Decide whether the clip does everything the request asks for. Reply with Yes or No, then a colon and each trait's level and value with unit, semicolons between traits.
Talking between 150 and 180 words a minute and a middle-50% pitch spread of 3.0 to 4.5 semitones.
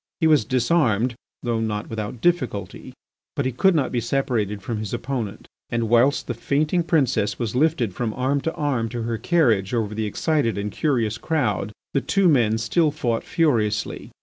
No: average, 175 wpm; average, 4.9 semitones